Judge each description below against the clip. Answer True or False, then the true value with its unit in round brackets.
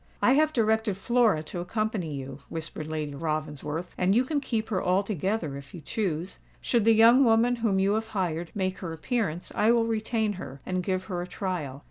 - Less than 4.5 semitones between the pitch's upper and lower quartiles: False (5.6 semitones)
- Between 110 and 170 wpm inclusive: False (195 wpm)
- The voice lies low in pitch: False (190 Hz)